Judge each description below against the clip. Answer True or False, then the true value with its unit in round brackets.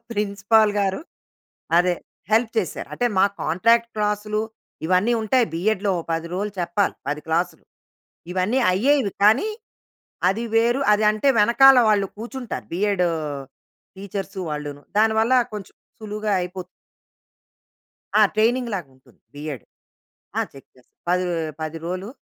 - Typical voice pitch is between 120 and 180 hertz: False (205 Hz)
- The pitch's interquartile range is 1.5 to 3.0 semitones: False (3.6 semitones)